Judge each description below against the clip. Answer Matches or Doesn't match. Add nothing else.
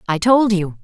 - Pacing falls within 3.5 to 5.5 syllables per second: Matches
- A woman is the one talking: Matches